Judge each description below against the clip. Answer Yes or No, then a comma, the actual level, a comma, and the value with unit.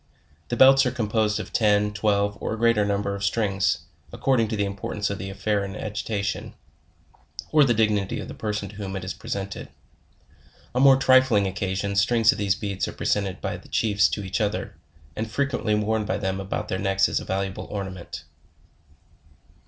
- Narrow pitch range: Yes, narrow, 2.1 semitones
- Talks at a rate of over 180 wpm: Yes, average, 190 wpm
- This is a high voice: No, low, 105 Hz